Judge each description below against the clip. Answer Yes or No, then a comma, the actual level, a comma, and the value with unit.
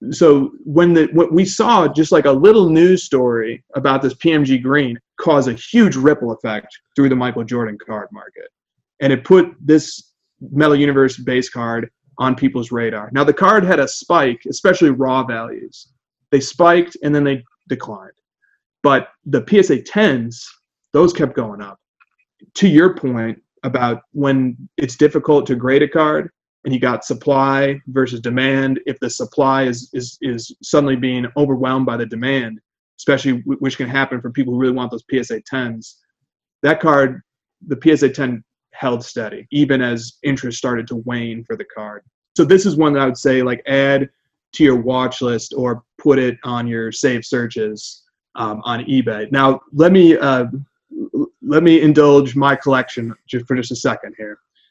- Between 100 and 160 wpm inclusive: No, average, 175 wpm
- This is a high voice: No, low, 135 Hz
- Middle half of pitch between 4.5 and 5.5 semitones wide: No, average, 3.0 semitones